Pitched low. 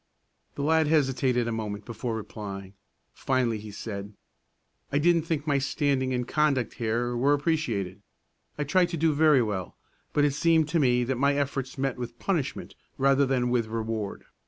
Yes: low, 130 Hz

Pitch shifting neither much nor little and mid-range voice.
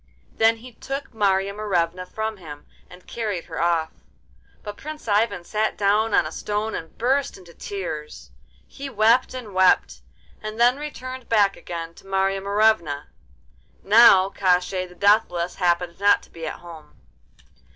No: average, 4.2 semitones; high, 200 Hz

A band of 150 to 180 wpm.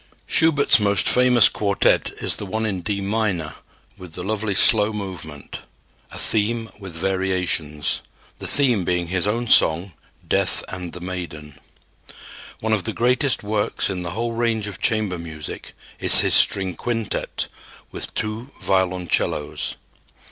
No: average, 140 wpm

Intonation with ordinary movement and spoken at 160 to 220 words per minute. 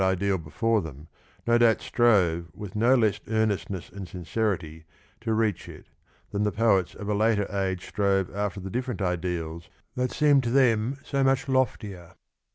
Yes: average, 3.9 semitones; average, 170 wpm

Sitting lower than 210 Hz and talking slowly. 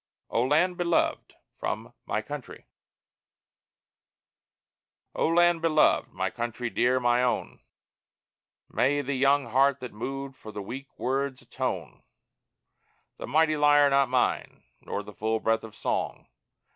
Yes: low, 135 Hz; slow, 130 wpm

